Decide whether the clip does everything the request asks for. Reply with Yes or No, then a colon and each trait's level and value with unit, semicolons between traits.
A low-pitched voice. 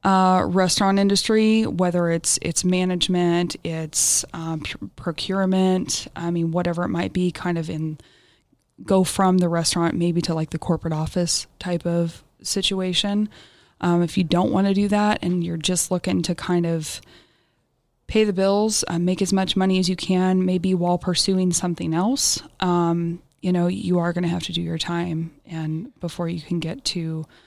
No: medium, 175 Hz